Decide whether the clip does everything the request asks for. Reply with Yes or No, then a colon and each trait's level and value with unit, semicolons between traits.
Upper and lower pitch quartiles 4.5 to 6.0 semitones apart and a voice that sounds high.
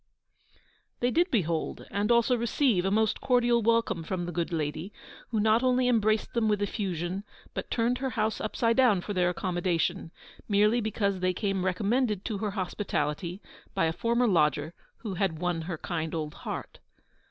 Yes: average, 4.8 semitones; high, 200 Hz